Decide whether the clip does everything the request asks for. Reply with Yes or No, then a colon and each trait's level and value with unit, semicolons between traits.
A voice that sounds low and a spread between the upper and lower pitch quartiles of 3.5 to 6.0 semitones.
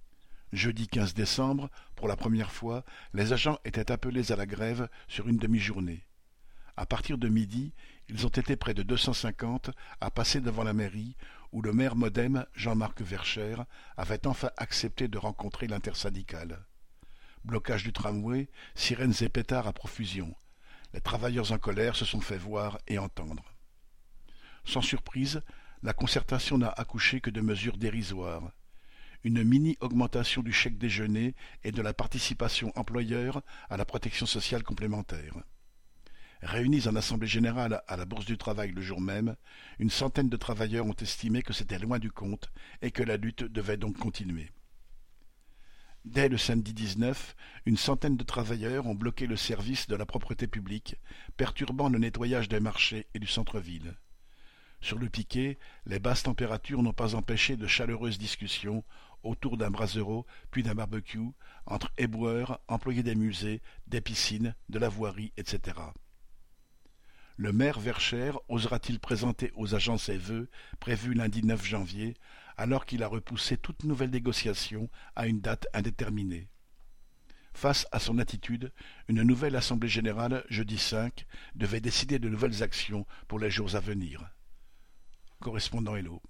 No: low, 115 Hz; average, 2.7 semitones